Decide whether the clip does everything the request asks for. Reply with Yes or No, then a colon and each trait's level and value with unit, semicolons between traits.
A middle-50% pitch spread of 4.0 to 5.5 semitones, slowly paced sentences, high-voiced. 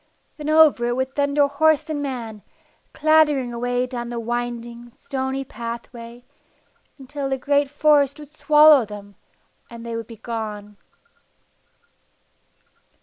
No: average, 3.5 semitones; slow, 125 wpm; very high, 255 Hz